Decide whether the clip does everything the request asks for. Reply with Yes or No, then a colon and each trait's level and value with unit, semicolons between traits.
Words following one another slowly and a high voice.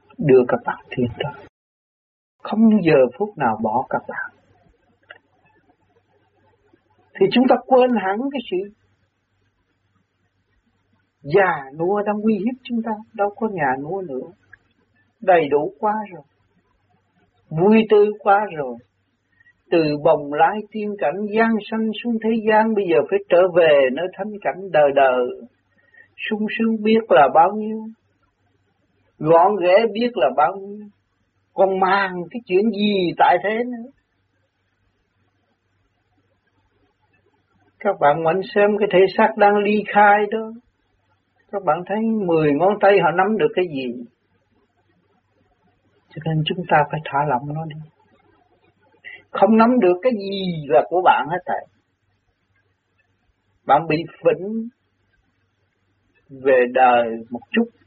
No: slow, 130 wpm; medium, 170 Hz